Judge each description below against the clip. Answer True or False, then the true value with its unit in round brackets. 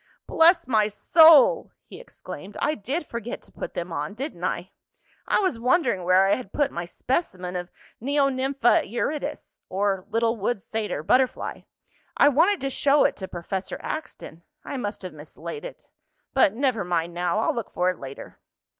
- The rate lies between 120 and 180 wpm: True (170 wpm)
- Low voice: False (230 Hz)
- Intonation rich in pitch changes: True (7.3 semitones)